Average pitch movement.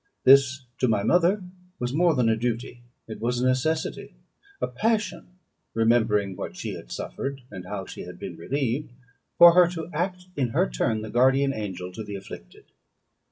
No: wide, 6.2 semitones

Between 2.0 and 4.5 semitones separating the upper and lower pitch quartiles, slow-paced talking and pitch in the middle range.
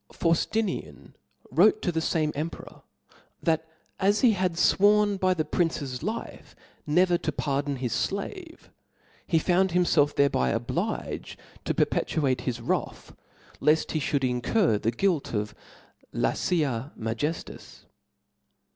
No: wide, 5.4 semitones; slow, 130 wpm; medium, 160 Hz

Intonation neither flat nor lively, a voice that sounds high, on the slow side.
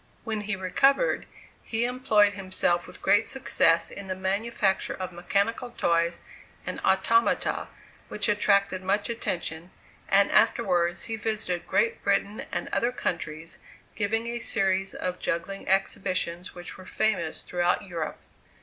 Yes: average, 3.6 semitones; high, 195 Hz; slow, 130 wpm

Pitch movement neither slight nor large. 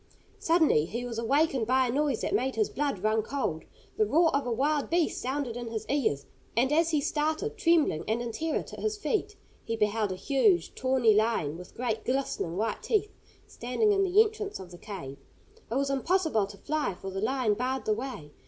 No: wide, 6.2 semitones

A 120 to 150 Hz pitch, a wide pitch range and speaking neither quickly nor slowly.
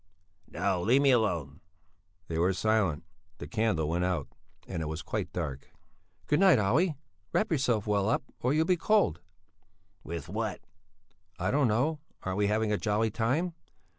No: low, 105 Hz; wide, 7.1 semitones; average, 165 wpm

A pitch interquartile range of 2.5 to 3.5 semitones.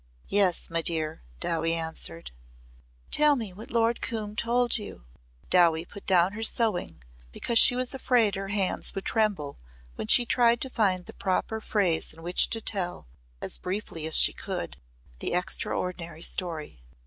No: average, 5.2 semitones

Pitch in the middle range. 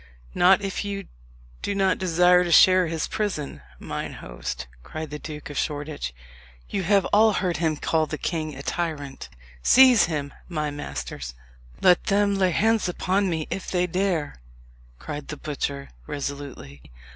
Yes: medium, 165 Hz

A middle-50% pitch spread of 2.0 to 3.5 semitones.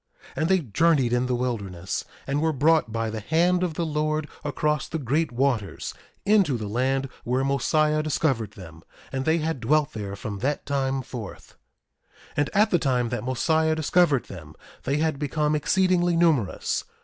No: average, 4.6 semitones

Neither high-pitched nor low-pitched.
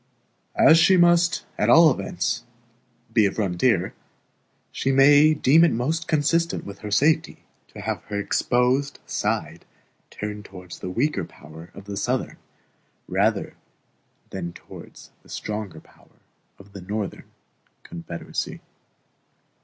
No: low, 115 Hz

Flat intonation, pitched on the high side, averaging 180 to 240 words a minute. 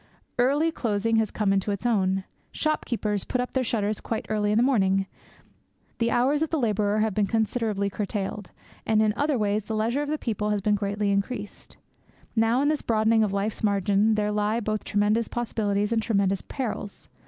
Yes: narrow, 2.3 semitones; high, 215 Hz; average, 190 wpm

